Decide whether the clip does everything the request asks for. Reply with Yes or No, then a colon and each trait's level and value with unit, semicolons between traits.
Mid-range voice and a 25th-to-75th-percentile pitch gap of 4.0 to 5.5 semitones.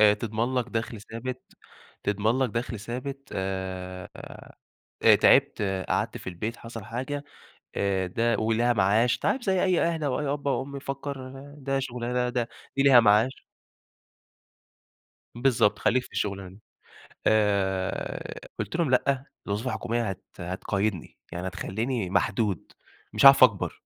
No: low, 115 Hz; average, 4.4 semitones